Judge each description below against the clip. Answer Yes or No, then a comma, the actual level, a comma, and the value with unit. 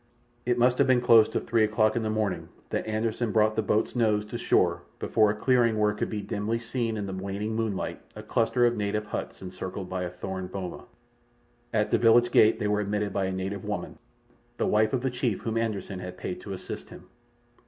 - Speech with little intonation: Yes, narrow, 2.3 semitones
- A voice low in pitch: Yes, low, 110 Hz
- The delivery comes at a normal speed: No, fast, 220 wpm